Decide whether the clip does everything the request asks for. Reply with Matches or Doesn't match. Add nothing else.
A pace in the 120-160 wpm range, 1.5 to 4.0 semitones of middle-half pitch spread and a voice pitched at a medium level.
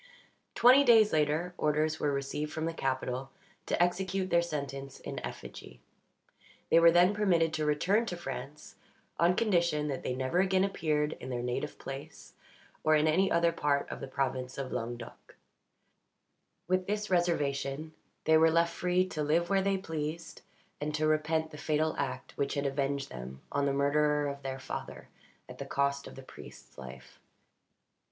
Doesn't match